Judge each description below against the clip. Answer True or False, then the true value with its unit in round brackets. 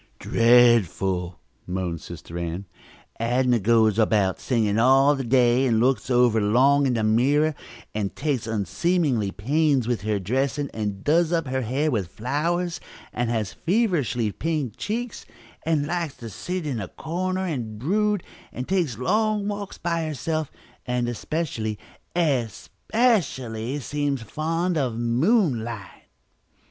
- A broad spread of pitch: True (6.2 semitones)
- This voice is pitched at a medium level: False (130 Hz)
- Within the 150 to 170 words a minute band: False (135 wpm)